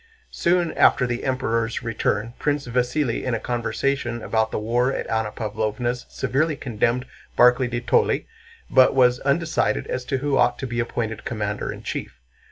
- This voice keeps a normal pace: Yes, average, 165 wpm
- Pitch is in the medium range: No, low, 120 Hz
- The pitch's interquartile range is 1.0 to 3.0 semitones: Yes, average, 2.7 semitones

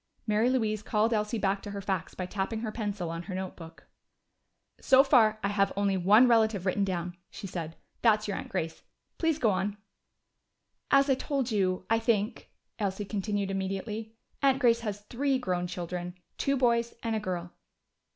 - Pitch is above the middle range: Yes, high, 210 Hz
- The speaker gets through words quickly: No, average, 175 wpm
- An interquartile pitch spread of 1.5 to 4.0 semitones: Yes, average, 3.4 semitones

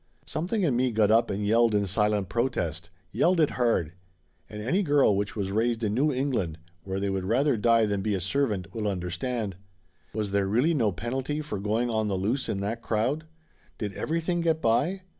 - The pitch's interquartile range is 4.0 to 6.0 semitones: Yes, average, 4.9 semitones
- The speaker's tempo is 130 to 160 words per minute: No, average, 195 wpm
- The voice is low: Yes, low, 110 Hz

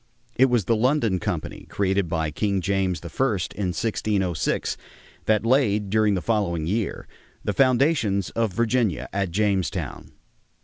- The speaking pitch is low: Yes, low, 100 Hz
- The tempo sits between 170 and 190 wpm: No, slow, 135 wpm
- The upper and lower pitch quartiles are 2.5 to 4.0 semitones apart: Yes, average, 3.7 semitones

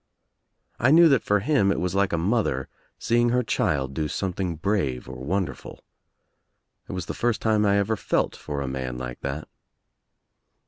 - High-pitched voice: No, very low, 95 Hz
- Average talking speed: Yes, average, 180 wpm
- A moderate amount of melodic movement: No, wide, 7.8 semitones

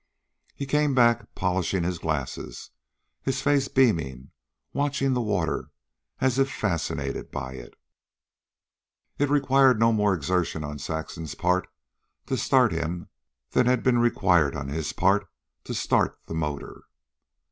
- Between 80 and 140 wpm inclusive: Yes, slow, 135 wpm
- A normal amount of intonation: No, wide, 8.2 semitones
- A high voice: No, very low, 95 Hz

